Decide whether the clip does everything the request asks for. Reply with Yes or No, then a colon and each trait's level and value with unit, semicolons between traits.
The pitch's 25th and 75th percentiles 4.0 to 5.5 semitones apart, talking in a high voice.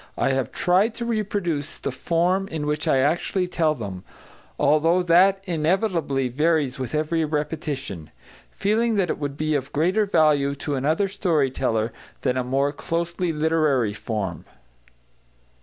No: average, 4.4 semitones; medium, 155 Hz